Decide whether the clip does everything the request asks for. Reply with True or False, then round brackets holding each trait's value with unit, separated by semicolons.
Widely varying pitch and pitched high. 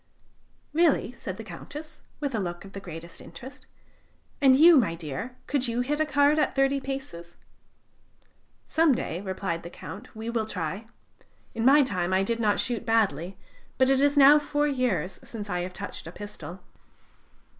True (6.9 semitones; 225 Hz)